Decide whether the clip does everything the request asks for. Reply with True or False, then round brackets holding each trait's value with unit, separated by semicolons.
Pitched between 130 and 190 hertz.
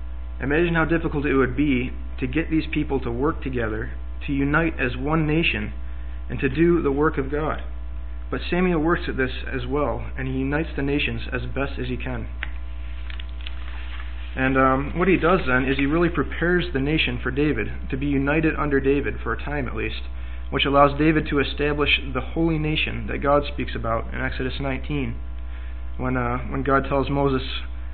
True (135 Hz)